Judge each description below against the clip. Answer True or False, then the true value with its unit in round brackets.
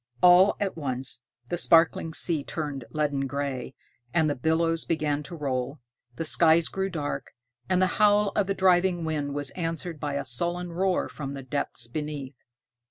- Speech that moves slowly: False (165 wpm)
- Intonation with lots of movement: False (3.8 semitones)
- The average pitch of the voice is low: False (160 Hz)